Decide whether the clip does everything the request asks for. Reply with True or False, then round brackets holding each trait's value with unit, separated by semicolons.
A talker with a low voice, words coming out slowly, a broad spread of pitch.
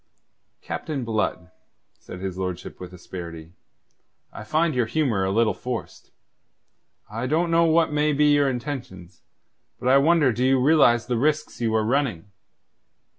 False (125 Hz; 150 wpm; 6.9 semitones)